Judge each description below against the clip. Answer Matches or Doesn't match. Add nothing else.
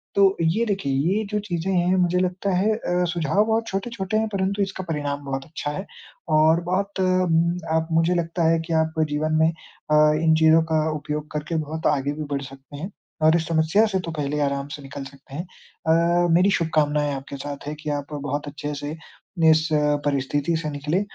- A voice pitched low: Doesn't match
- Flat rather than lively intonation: Doesn't match